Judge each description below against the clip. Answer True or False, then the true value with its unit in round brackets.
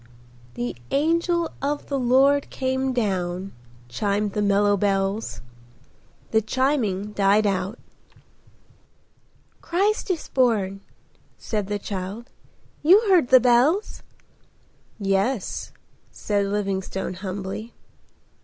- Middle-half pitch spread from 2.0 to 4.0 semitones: False (5.1 semitones)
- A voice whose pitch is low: False (210 Hz)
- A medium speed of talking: False (90 wpm)